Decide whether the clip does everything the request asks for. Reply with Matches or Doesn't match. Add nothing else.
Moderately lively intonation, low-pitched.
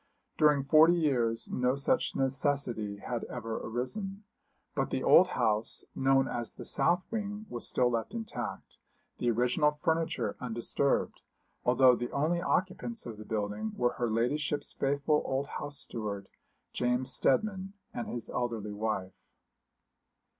Matches